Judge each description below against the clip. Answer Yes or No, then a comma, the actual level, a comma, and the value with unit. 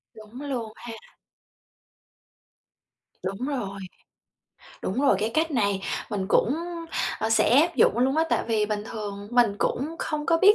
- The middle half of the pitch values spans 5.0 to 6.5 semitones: Yes, average, 5.3 semitones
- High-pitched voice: Yes, high, 230 Hz